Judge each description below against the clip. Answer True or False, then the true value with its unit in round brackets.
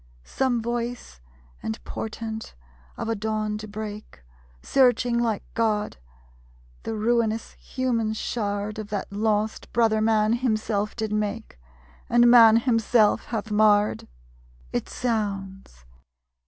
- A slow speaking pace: True (115 wpm)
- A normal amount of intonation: False (1.7 semitones)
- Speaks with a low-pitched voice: False (220 Hz)